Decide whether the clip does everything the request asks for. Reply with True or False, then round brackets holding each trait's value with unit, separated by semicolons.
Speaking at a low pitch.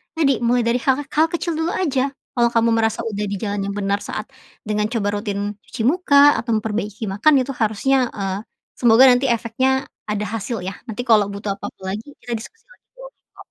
False (230 Hz)